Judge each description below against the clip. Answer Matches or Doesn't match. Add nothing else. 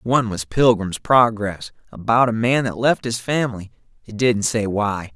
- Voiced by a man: Matches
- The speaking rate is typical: Matches